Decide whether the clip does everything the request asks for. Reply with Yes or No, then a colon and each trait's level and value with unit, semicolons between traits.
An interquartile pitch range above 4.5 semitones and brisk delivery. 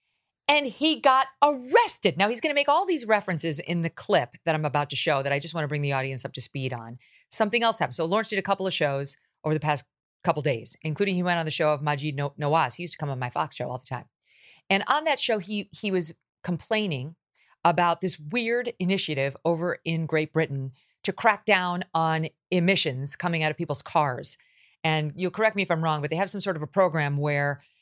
Yes: average, 5.1 semitones; fast, 235 wpm